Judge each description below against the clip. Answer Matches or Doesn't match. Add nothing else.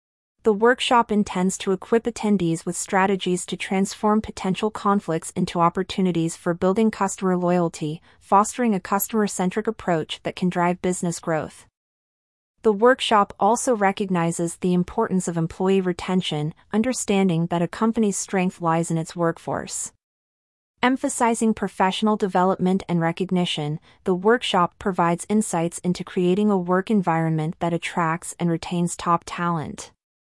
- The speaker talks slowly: Matches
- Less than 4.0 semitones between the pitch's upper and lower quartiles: Matches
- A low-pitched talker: Doesn't match